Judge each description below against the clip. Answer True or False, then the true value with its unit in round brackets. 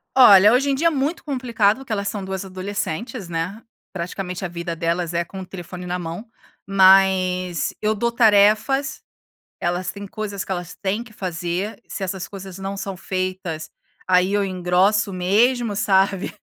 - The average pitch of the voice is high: True (195 Hz)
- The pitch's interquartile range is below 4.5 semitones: True (2.8 semitones)